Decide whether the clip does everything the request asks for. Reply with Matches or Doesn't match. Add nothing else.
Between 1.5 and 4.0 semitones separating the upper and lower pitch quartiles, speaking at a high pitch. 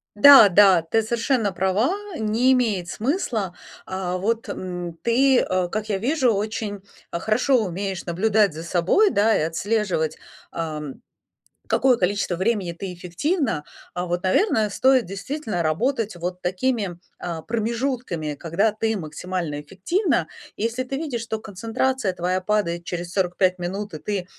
Doesn't match